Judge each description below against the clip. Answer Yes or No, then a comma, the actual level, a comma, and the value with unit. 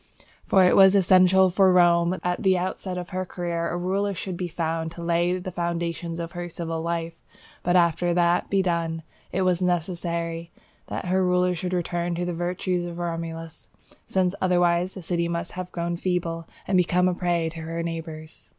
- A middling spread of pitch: No, narrow, 1.3 semitones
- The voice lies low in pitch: No, medium, 175 Hz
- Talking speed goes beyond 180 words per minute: Yes, average, 195 wpm